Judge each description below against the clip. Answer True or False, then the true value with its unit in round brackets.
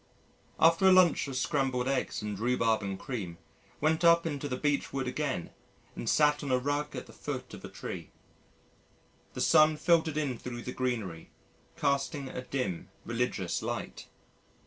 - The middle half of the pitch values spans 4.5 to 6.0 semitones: False (3.8 semitones)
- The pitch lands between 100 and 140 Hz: True (135 Hz)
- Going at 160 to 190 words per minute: True (165 wpm)